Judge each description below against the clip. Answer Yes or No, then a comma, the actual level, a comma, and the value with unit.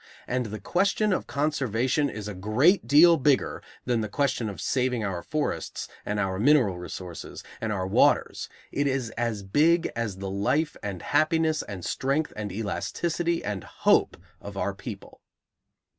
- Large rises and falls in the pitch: Yes, wide, 6.6 semitones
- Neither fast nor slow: Yes, average, 160 wpm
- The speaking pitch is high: No, low, 120 Hz